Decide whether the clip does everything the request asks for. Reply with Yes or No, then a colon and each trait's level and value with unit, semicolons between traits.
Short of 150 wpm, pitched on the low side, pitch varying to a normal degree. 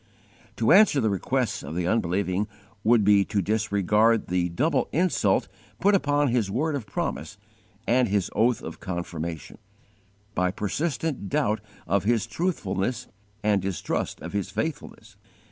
Yes: average, 140 wpm; low, 105 Hz; average, 4.9 semitones